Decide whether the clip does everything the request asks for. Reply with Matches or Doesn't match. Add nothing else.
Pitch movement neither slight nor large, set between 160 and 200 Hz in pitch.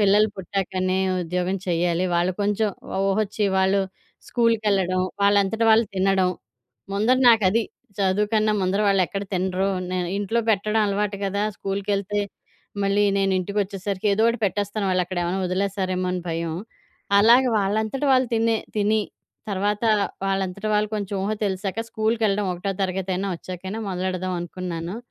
Doesn't match